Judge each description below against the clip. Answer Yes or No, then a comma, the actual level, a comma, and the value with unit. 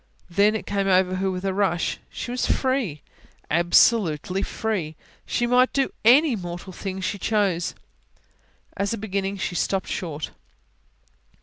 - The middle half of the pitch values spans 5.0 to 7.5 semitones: No, average, 3.3 semitones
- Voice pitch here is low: No, high, 195 Hz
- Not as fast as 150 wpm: Yes, average, 140 wpm